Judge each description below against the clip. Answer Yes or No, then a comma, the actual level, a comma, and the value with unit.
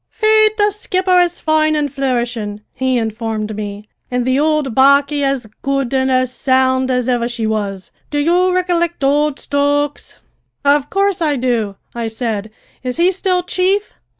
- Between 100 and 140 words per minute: No, average, 160 wpm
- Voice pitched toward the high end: Yes, very high, 275 Hz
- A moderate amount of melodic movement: No, wide, 5.9 semitones